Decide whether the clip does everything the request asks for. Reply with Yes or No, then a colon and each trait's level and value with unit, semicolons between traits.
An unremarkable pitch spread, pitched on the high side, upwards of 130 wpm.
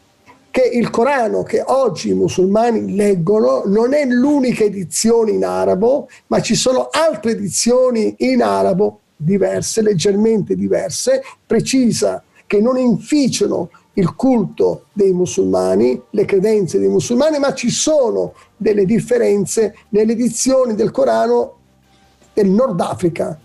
No: average, 4.0 semitones; high, 215 Hz; average, 125 wpm